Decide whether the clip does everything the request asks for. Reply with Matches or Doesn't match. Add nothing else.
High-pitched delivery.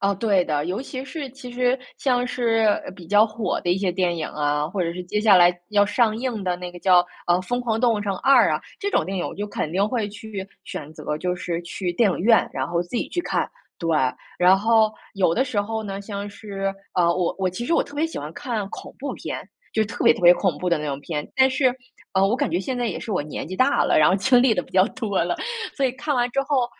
Matches